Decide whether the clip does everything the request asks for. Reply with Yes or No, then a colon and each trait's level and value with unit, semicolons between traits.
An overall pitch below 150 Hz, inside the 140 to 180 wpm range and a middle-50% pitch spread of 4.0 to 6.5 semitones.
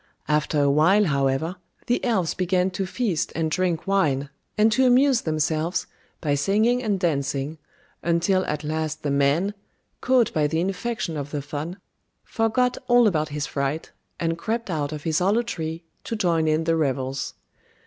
No: medium, 165 Hz; average, 165 wpm; average, 4.9 semitones